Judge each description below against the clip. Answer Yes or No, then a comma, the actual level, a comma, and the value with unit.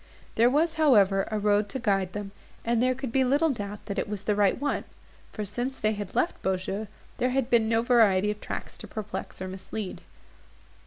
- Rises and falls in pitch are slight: No, average, 3.7 semitones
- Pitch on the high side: Yes, high, 215 Hz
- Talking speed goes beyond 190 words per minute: Yes, fast, 205 wpm